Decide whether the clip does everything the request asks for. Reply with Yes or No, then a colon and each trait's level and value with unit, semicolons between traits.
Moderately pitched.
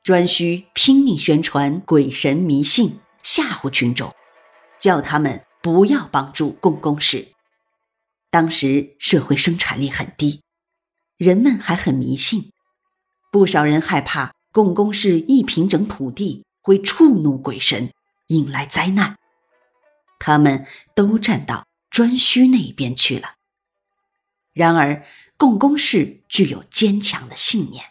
Yes: medium, 180 Hz